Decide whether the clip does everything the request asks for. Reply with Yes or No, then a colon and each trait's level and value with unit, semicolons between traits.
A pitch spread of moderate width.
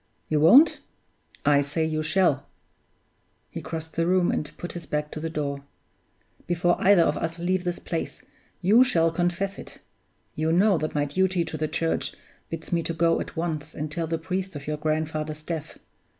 No: narrow, 2.3 semitones